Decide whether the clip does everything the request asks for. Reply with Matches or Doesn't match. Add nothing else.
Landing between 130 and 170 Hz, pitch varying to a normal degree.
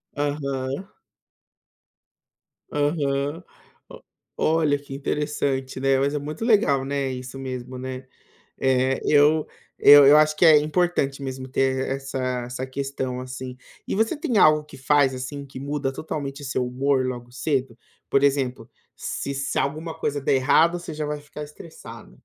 Doesn't match